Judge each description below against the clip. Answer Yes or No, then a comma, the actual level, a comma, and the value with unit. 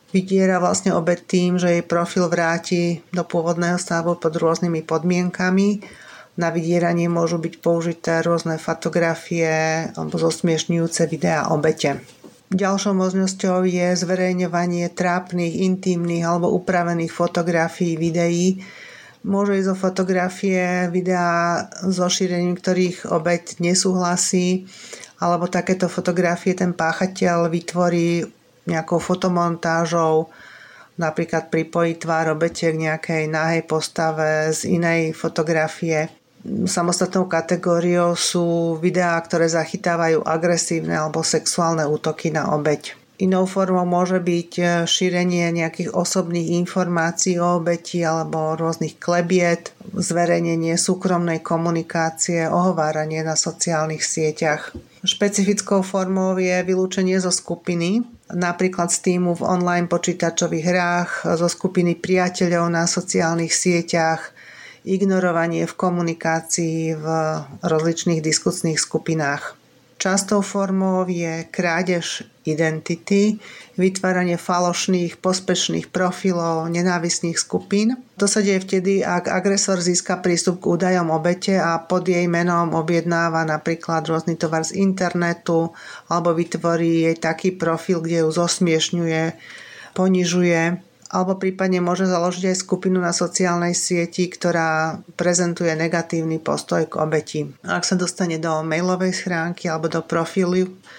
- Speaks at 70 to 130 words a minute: Yes, slow, 110 wpm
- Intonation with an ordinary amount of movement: No, narrow, 1.8 semitones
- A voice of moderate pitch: Yes, medium, 175 Hz